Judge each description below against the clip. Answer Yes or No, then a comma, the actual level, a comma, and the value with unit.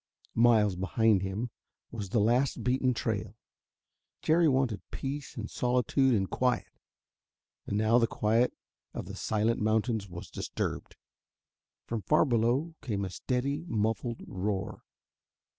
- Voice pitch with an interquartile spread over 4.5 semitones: No, average, 3.1 semitones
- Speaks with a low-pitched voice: Yes, low, 115 Hz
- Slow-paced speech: Yes, slow, 125 wpm